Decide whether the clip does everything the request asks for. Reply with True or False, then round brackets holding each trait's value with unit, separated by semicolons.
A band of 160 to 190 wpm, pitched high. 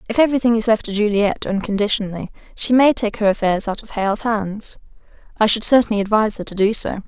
False (205 wpm; 215 Hz)